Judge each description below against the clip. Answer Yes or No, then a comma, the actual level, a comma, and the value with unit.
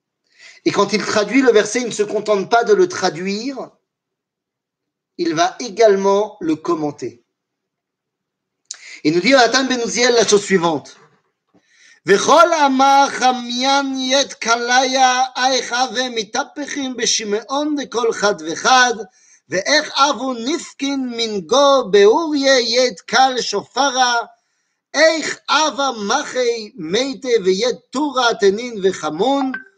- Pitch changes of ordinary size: Yes, average, 4.3 semitones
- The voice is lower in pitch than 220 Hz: No, very high, 255 Hz